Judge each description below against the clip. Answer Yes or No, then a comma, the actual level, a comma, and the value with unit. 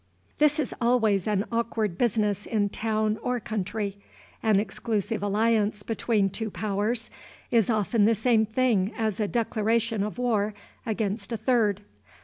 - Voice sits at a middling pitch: No, high, 220 Hz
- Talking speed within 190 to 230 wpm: No, average, 140 wpm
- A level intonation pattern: Yes, narrow, 2.0 semitones